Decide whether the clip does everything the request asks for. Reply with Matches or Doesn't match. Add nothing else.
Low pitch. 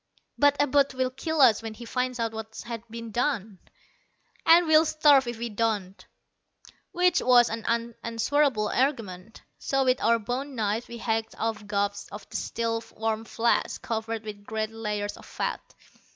Doesn't match